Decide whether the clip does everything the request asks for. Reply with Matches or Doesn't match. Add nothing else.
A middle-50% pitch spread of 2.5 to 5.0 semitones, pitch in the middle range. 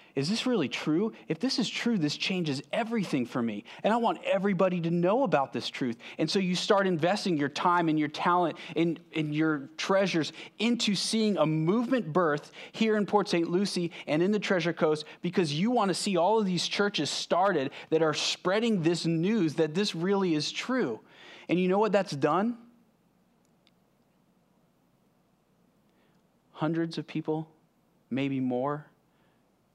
Matches